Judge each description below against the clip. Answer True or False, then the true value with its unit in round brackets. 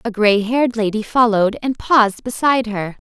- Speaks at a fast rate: False (175 wpm)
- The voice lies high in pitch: True (225 Hz)